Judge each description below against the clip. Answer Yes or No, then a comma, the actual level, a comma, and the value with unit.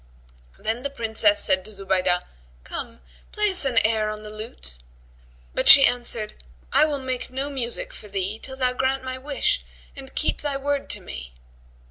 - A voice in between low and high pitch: No, high, 245 Hz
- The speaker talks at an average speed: Yes, average, 175 wpm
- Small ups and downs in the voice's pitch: No, average, 4.5 semitones